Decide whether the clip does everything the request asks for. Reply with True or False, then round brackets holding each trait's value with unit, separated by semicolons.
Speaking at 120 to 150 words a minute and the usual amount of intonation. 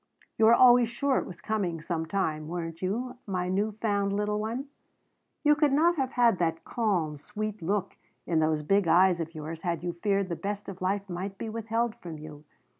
False (200 wpm; 4.6 semitones)